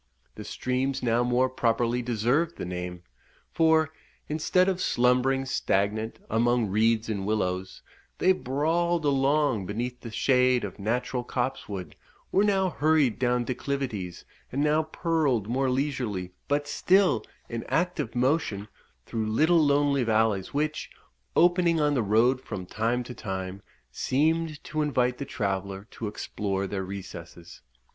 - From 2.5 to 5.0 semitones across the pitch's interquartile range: No, wide, 5.4 semitones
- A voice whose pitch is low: Yes, low, 125 Hz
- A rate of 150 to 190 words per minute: No, slow, 135 wpm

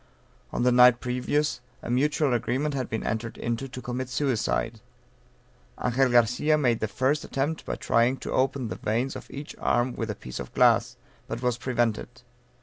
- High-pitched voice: No, low, 125 Hz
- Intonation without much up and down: Yes, narrow, 2.3 semitones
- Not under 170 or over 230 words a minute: Yes, average, 175 wpm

